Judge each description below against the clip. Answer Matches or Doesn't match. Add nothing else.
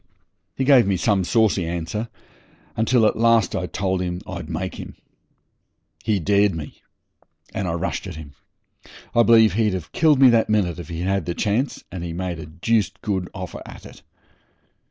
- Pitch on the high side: Doesn't match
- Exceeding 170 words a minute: Matches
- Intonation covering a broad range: Doesn't match